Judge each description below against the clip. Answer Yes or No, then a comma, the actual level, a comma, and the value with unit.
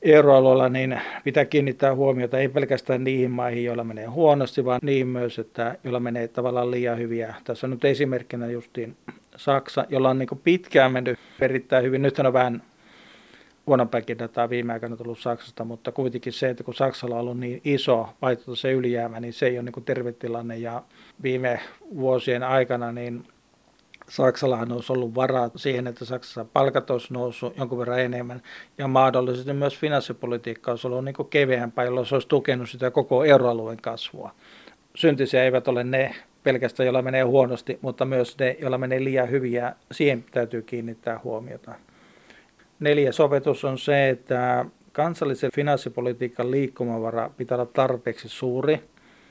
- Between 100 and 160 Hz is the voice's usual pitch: Yes, low, 125 Hz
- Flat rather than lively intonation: Yes, narrow, 1.7 semitones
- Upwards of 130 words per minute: Yes, fast, 155 wpm